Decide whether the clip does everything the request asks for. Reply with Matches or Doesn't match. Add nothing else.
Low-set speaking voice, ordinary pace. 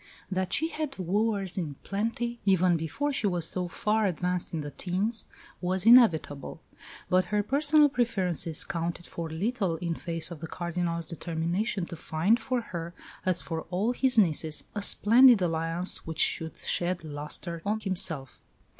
Doesn't match